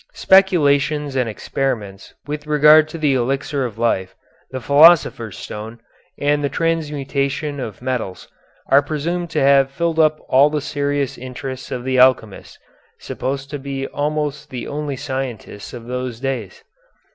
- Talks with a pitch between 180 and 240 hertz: No, medium, 140 Hz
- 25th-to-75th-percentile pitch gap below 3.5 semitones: Yes, average, 2.9 semitones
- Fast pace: No, average, 145 wpm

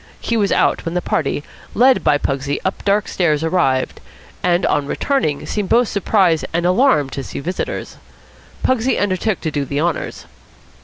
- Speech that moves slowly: No, average, 165 wpm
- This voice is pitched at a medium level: Yes, medium, 175 Hz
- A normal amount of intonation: No, wide, 6.0 semitones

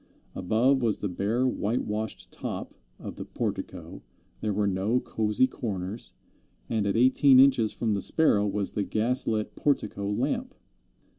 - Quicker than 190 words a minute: No, average, 150 wpm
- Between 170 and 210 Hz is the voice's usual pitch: No, low, 110 Hz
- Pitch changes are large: No, average, 3.8 semitones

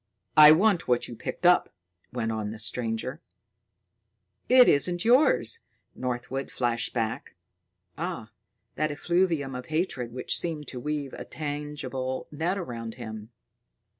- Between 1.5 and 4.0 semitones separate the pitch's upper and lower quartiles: No, average, 5.2 semitones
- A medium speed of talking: No, slow, 130 wpm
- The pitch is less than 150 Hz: Yes, low, 135 Hz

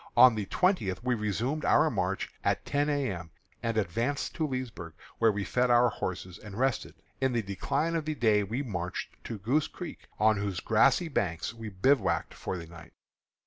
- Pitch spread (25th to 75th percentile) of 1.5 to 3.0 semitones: No, wide, 5.4 semitones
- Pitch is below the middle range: Yes, low, 115 Hz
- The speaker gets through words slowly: No, average, 185 wpm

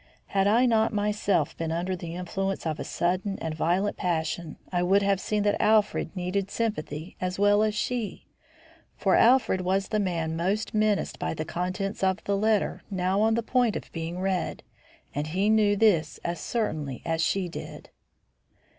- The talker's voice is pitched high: Yes, high, 195 Hz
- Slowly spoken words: No, average, 175 wpm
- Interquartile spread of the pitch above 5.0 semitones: No, average, 3.4 semitones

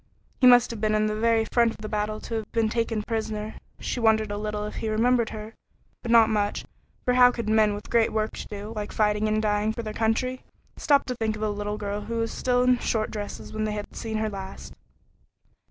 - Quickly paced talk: Yes, fast, 235 wpm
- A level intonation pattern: Yes, narrow, 1.5 semitones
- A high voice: Yes, high, 220 Hz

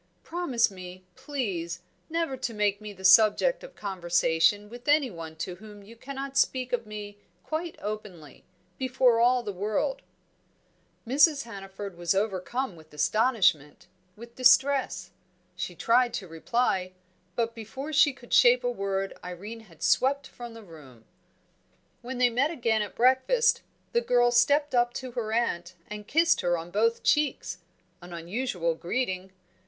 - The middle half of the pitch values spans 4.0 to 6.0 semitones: Yes, wide, 5.5 semitones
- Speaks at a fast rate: No, average, 150 wpm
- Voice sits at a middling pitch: No, high, 225 Hz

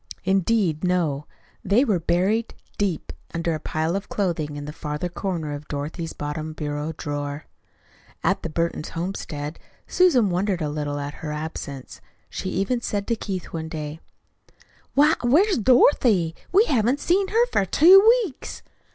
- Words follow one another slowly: No, average, 150 wpm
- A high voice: No, medium, 170 Hz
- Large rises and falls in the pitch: Yes, wide, 6.2 semitones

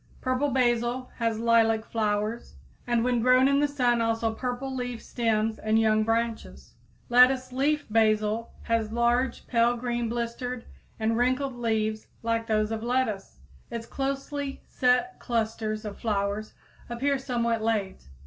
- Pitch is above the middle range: Yes, high, 235 Hz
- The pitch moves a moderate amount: No, narrow, 2.2 semitones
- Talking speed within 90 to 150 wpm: Yes, average, 140 wpm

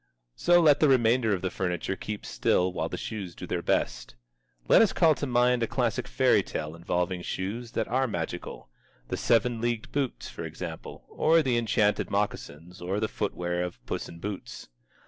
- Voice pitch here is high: No, low, 105 Hz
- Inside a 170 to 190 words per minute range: Yes, average, 185 wpm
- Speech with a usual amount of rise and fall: No, wide, 5.7 semitones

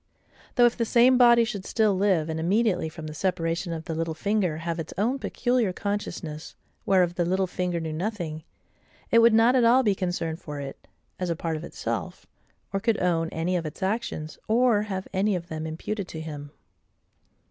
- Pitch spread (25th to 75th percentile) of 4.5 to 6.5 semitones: Yes, average, 4.9 semitones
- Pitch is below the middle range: No, medium, 180 Hz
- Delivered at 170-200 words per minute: Yes, average, 195 wpm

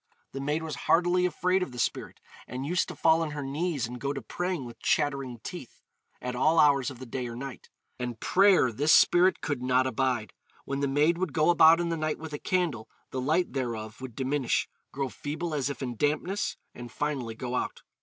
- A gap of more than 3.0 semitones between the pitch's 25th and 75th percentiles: Yes, average, 4.3 semitones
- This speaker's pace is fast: Yes, fast, 215 wpm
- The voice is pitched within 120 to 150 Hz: Yes, medium, 140 Hz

